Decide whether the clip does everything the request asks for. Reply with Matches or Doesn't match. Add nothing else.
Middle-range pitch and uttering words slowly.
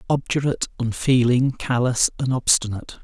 Doesn't match